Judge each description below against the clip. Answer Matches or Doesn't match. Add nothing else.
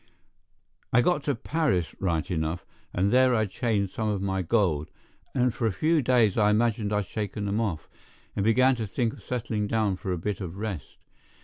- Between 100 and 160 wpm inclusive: Doesn't match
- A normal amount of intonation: Matches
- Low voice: Matches